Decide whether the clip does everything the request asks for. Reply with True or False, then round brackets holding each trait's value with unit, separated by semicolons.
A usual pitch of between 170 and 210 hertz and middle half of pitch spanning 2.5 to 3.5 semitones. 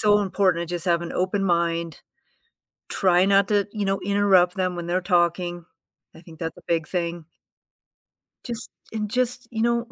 True (185 Hz; 2.9 semitones)